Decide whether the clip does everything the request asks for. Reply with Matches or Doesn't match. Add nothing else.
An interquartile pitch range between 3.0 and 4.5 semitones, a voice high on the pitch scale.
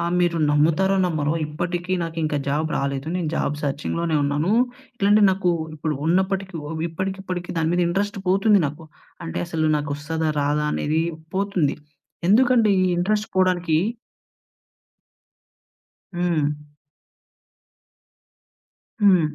Doesn't match